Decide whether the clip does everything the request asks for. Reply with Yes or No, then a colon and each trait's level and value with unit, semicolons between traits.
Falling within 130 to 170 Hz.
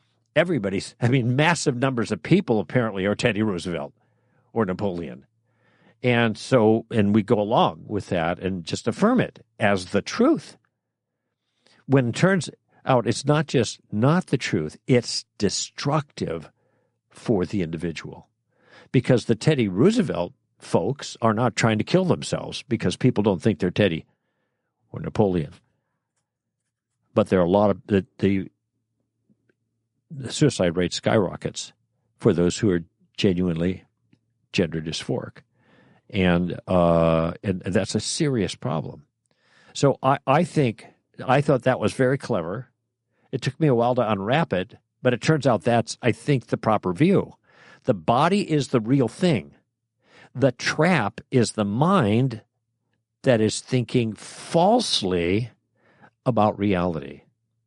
No: low, 115 Hz